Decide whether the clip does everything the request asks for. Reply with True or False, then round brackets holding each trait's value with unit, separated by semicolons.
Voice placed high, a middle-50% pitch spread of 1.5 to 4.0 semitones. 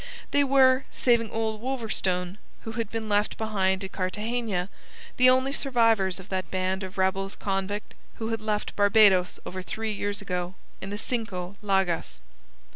True (205 Hz; 3.1 semitones)